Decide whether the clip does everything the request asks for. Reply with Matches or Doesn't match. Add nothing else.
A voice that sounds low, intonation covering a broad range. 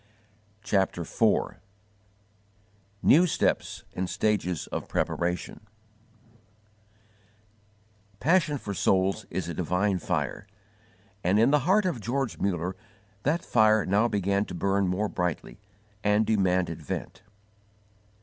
Doesn't match